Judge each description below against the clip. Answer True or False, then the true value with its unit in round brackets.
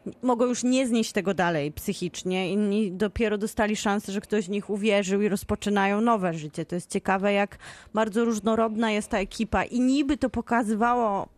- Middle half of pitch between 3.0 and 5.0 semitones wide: False (2.5 semitones)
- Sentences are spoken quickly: True (175 wpm)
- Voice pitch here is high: True (210 Hz)